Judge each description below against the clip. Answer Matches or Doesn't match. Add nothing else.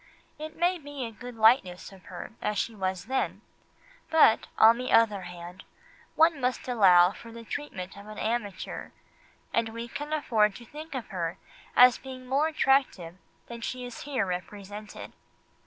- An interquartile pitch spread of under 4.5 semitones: Doesn't match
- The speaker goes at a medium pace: Matches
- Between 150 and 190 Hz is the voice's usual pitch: Doesn't match